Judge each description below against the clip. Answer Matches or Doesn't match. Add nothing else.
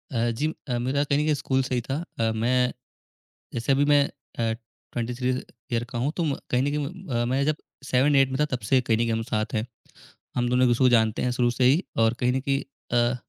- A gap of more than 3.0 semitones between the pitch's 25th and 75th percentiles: Doesn't match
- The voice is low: Matches